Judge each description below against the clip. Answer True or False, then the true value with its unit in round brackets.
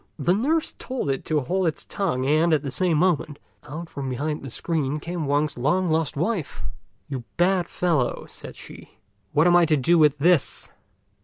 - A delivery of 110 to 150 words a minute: False (185 wpm)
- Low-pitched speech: False (155 Hz)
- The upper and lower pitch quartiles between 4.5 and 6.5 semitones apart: False (3.6 semitones)